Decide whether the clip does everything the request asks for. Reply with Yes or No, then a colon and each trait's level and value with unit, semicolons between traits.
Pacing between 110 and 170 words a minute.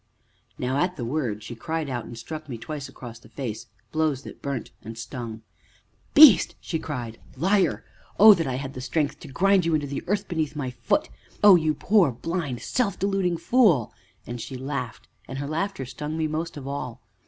No: average, 195 wpm